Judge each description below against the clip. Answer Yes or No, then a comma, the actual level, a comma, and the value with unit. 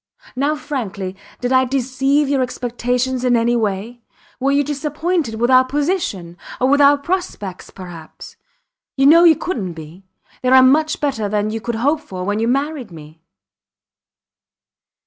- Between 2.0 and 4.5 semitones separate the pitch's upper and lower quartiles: No, average, 5.2 semitones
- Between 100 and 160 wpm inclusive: Yes, average, 155 wpm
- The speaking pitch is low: No, very high, 255 Hz